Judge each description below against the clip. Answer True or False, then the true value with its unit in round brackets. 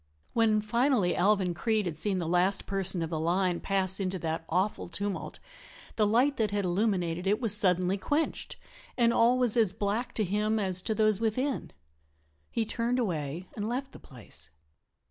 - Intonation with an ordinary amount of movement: True (3.8 semitones)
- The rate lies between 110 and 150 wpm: False (175 wpm)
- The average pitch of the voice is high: True (200 Hz)